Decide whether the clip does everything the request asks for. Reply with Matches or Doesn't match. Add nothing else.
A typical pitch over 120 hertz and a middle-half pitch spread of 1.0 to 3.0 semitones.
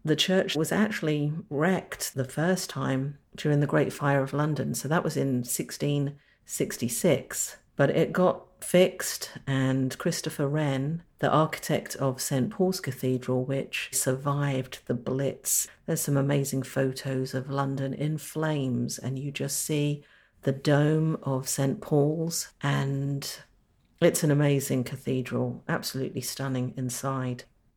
Matches